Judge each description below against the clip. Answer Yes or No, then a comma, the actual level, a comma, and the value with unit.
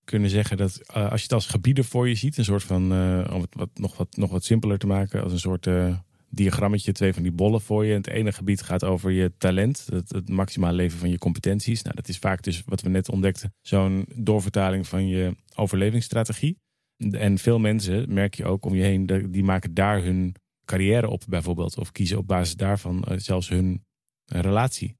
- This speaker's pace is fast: Yes, fast, 220 wpm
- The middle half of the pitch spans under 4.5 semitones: Yes, narrow, 2.4 semitones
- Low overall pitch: Yes, very low, 95 Hz